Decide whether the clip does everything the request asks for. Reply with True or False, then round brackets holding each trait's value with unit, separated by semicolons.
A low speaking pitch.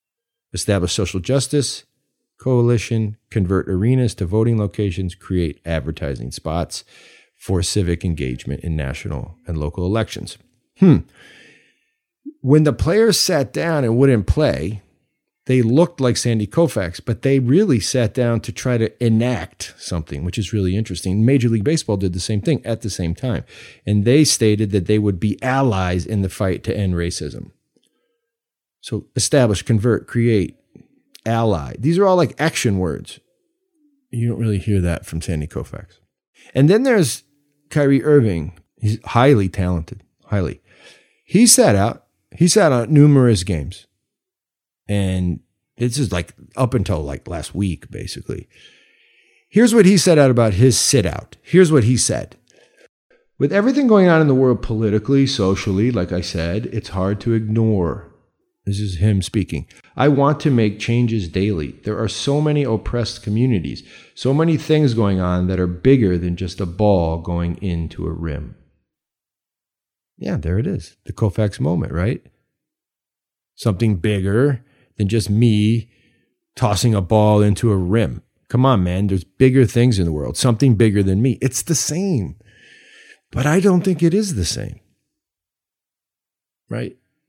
True (110 Hz)